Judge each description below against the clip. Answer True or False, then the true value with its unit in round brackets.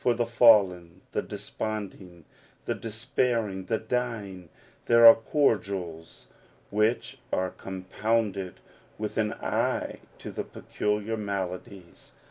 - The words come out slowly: True (105 wpm)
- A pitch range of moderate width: True (3.5 semitones)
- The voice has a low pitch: True (105 Hz)